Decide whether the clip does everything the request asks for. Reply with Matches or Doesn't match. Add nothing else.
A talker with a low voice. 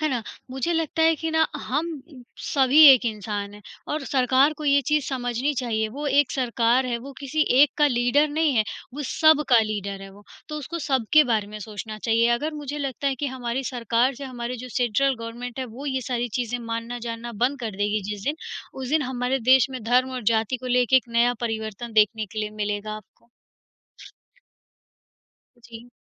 Doesn't match